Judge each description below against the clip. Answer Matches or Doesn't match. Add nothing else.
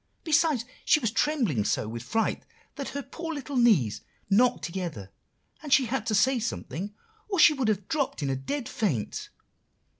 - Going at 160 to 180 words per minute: Matches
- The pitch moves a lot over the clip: Matches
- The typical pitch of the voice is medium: Doesn't match